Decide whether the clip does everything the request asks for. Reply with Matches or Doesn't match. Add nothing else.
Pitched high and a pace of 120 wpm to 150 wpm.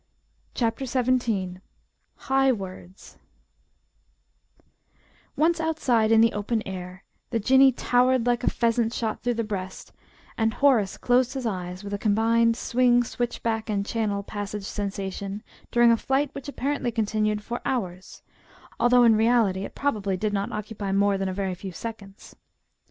Matches